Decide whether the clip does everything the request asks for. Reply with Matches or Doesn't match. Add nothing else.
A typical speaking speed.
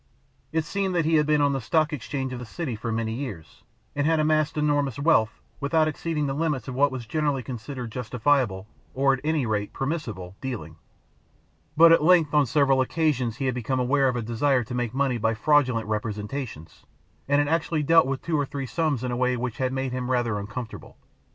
Doesn't match